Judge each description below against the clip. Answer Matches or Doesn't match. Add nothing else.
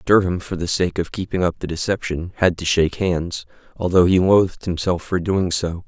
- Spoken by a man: Matches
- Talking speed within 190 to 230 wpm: Matches